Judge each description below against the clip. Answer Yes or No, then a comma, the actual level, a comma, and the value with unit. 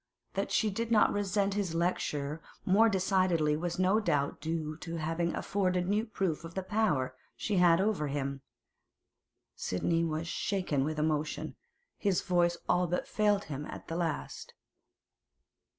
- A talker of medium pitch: Yes, medium, 175 Hz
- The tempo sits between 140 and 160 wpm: Yes, average, 150 wpm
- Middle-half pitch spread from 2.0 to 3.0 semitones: No, average, 4.0 semitones